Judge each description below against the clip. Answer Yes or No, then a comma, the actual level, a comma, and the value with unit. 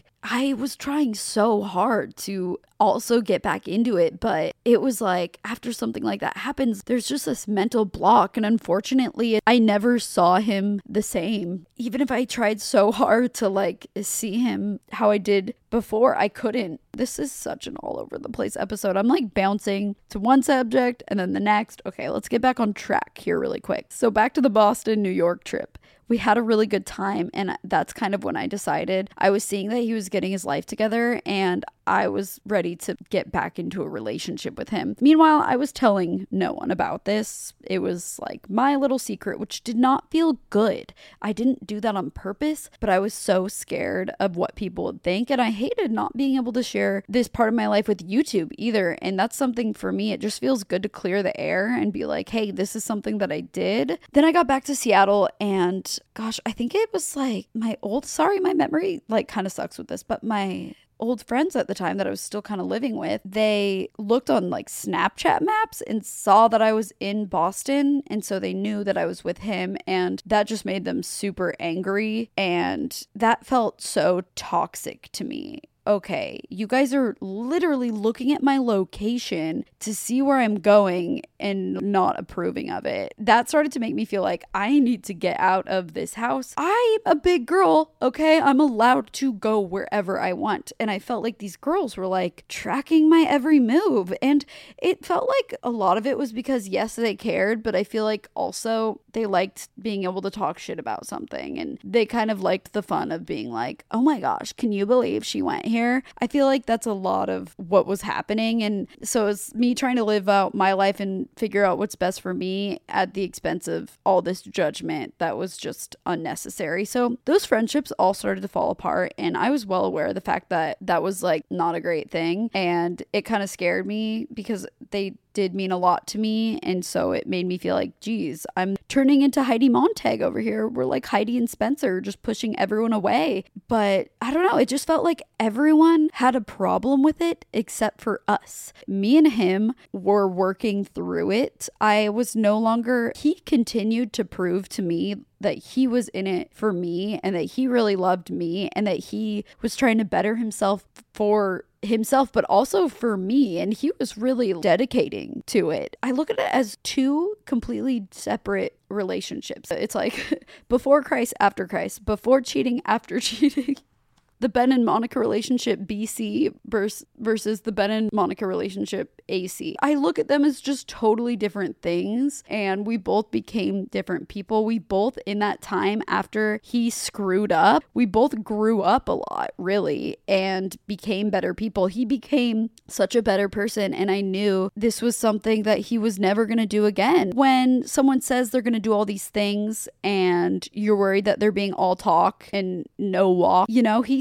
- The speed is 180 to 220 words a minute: Yes, average, 200 wpm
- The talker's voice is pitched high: Yes, high, 220 Hz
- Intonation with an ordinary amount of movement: Yes, average, 4.4 semitones